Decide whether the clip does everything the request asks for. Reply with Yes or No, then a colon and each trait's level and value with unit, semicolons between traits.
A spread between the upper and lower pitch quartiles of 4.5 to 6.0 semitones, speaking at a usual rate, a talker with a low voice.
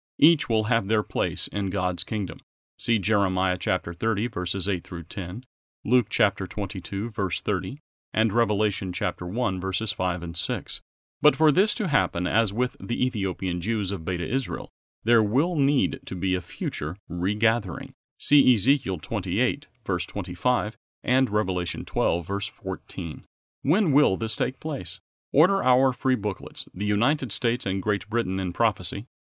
Yes: average, 4.8 semitones; average, 160 wpm; low, 105 Hz